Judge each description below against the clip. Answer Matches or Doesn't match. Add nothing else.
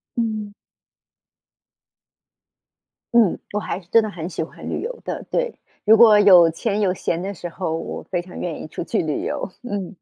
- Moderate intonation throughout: Matches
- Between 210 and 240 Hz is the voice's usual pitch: Doesn't match